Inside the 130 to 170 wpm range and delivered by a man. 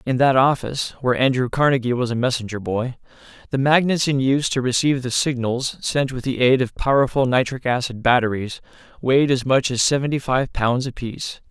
No: average, 185 wpm; male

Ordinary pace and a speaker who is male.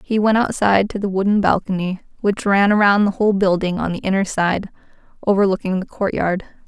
No: average, 180 wpm; female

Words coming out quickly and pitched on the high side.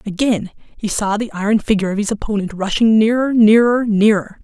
No: average, 175 wpm; high, 215 Hz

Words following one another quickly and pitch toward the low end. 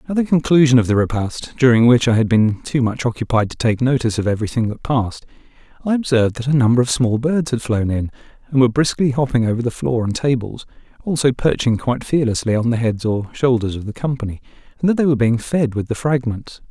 Yes: fast, 225 wpm; low, 125 Hz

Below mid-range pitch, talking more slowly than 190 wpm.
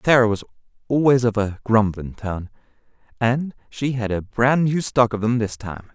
Yes: low, 115 Hz; average, 180 wpm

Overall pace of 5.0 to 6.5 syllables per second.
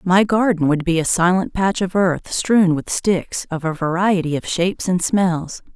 No: 4.4 syllables/s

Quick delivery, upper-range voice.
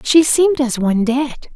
No: average, 190 wpm; very high, 270 Hz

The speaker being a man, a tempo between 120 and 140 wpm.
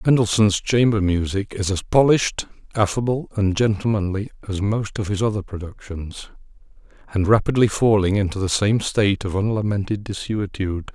Yes: male; slow, 135 wpm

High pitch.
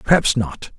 No: low, 130 Hz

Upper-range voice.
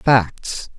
No: low, 110 Hz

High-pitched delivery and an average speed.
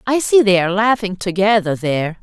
Yes: high, 200 Hz; average, 190 wpm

